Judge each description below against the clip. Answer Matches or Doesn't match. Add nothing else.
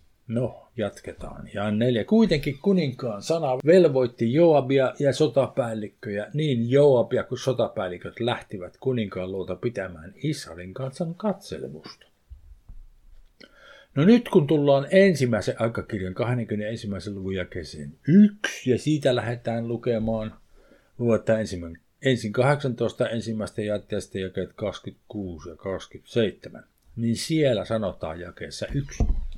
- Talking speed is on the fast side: Doesn't match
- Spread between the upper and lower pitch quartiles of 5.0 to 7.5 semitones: Matches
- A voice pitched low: Matches